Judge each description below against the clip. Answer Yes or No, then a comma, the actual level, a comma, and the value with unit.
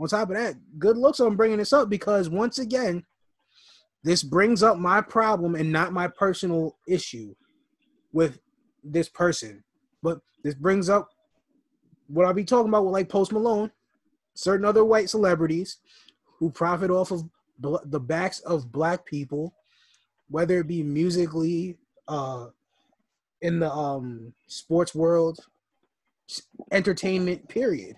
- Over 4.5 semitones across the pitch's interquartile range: Yes, average, 5.2 semitones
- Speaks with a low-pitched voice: No, medium, 185 Hz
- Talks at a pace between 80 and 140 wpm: Yes, slow, 135 wpm